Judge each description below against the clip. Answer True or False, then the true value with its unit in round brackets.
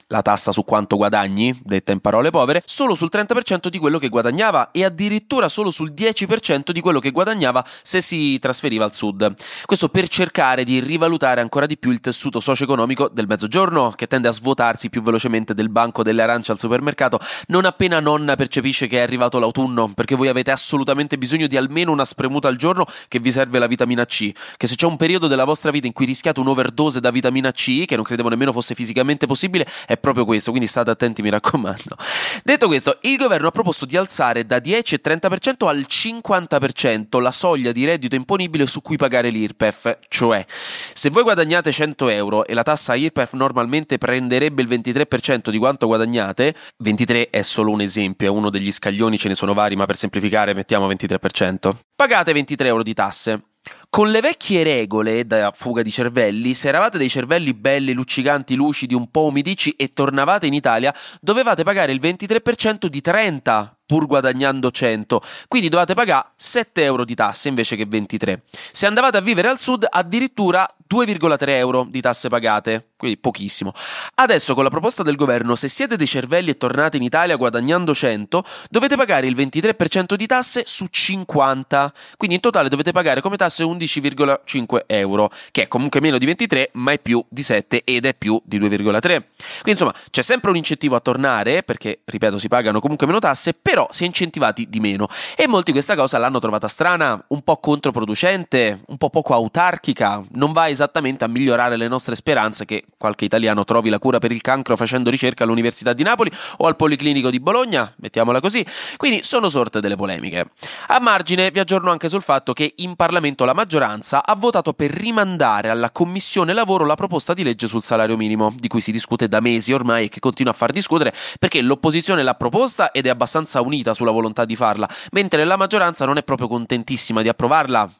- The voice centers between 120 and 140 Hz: True (135 Hz)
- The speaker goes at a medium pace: False (190 wpm)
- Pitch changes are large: True (6.0 semitones)